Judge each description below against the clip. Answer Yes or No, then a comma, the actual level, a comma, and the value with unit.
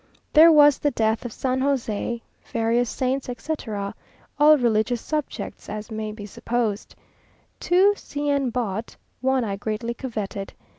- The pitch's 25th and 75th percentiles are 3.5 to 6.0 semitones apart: Yes, average, 4.1 semitones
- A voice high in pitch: Yes, high, 240 Hz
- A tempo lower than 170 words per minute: Yes, average, 140 wpm